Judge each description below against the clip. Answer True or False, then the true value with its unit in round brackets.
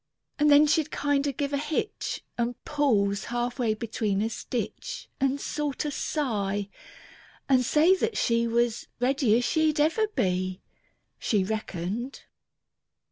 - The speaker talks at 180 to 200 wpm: False (135 wpm)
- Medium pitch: False (245 Hz)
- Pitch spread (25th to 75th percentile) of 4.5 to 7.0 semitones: True (5.2 semitones)